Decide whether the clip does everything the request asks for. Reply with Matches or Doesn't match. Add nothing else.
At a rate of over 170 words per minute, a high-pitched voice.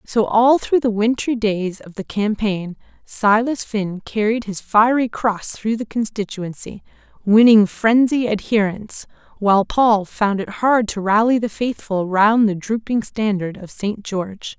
Doesn't match